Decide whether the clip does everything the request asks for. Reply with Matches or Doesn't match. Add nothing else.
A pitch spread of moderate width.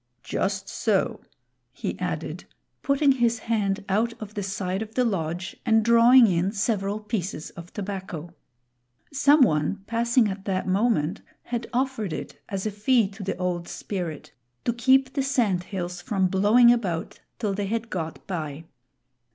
Matches